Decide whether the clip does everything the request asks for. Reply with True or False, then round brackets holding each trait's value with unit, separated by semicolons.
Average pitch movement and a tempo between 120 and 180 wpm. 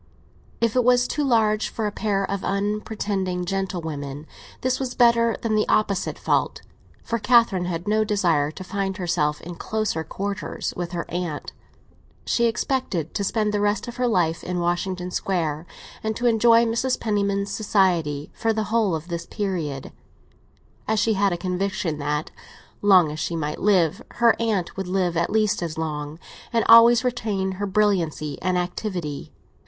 True (4.3 semitones; 165 wpm)